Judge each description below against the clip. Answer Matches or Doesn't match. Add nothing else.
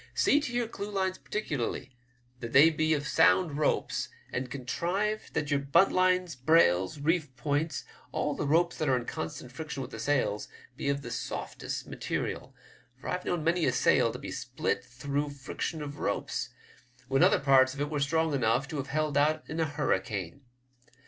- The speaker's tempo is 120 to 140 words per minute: Doesn't match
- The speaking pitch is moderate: Matches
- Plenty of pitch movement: Doesn't match